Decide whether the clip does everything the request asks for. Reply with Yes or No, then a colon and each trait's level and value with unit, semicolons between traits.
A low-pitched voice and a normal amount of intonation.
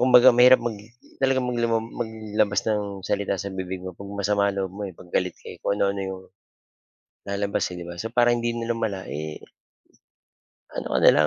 Yes: low, 100 Hz; average, 3.6 semitones